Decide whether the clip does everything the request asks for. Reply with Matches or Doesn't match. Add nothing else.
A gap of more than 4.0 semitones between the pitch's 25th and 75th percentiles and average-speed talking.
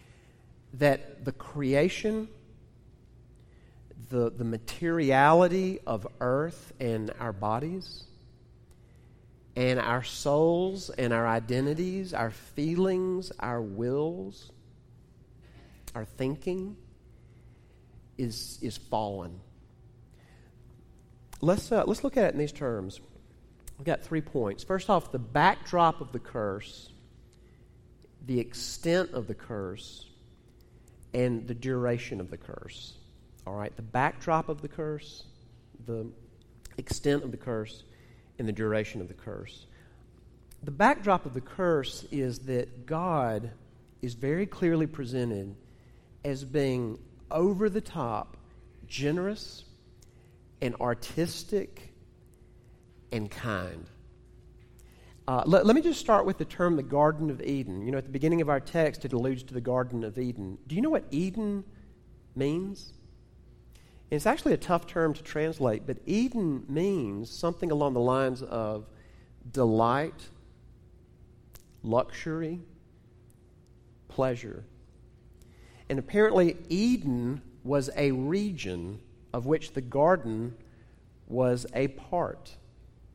Doesn't match